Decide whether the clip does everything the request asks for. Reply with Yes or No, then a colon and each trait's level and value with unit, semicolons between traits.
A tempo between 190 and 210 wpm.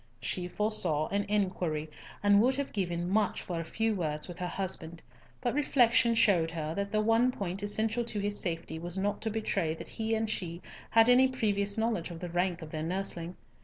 Yes: average, 200 wpm